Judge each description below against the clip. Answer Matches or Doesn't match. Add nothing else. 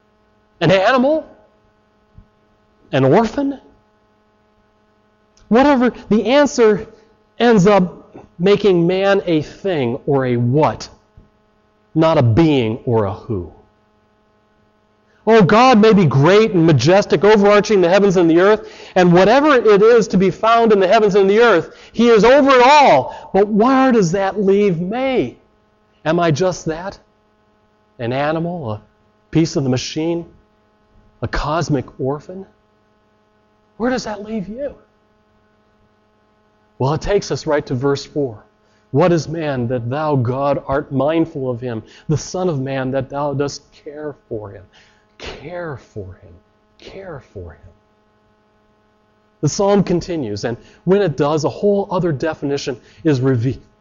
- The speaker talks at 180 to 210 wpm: Doesn't match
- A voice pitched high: Doesn't match